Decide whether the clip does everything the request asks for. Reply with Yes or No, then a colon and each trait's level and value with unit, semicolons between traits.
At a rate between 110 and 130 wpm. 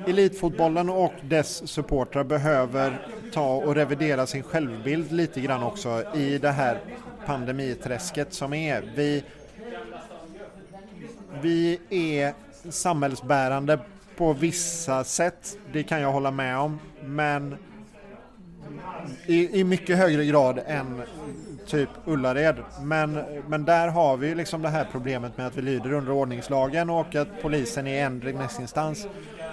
Yes: slow, 125 wpm